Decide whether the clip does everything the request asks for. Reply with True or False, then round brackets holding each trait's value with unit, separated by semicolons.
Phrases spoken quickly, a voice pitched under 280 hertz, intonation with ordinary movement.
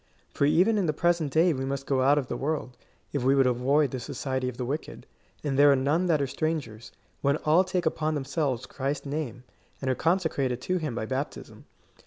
True (225 wpm; 140 Hz; 3.1 semitones)